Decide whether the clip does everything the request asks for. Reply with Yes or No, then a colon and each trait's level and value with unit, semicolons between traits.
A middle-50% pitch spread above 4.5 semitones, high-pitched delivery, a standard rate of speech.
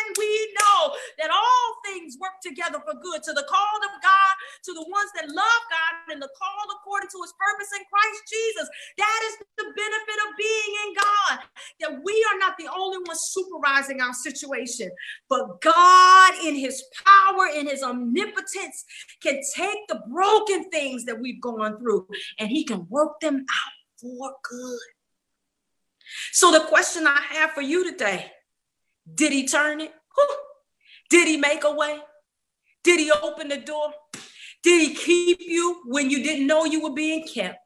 Yes: average, 5.1 semitones; very high, 325 Hz; average, 170 wpm